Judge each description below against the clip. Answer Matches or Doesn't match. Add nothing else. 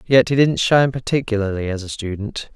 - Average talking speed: Matches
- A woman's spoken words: Doesn't match